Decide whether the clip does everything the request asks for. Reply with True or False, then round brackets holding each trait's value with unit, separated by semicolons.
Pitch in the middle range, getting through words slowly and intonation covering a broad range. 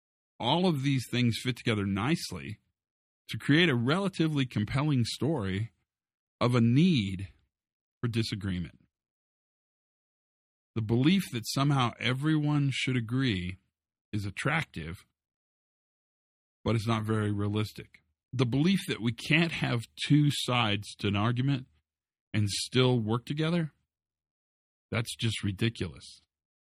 False (115 Hz; 115 wpm; 5.7 semitones)